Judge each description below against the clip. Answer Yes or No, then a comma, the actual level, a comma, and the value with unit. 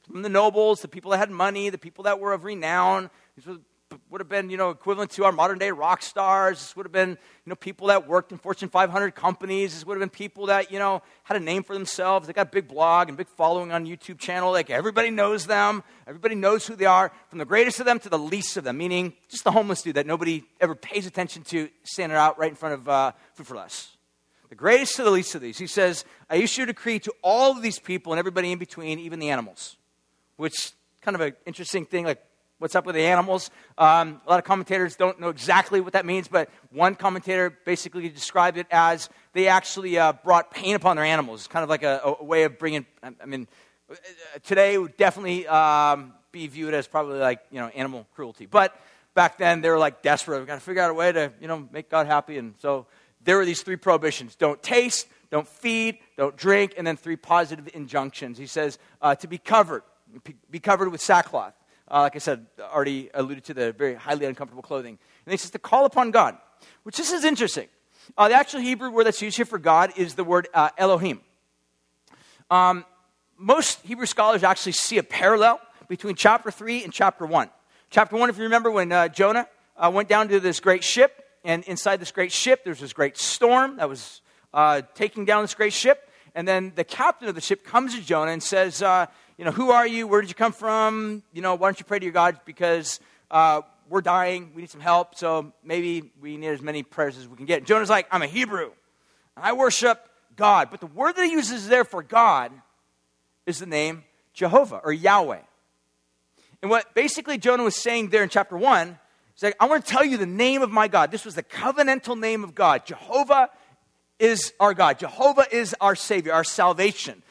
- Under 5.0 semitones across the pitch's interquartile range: Yes, average, 4.6 semitones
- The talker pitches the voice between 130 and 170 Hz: No, medium, 185 Hz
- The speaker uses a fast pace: Yes, fast, 225 wpm